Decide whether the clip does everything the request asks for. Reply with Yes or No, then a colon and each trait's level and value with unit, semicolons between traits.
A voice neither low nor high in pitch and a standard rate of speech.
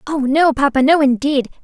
No: very high, 280 Hz; average, 185 wpm